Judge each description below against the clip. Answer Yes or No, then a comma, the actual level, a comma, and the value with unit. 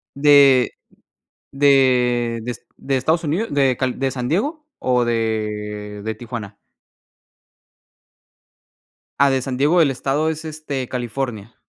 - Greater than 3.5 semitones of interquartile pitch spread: No, average, 3.2 semitones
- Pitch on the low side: Yes, low, 130 Hz